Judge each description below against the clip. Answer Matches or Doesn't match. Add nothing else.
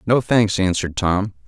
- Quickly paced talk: Doesn't match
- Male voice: Matches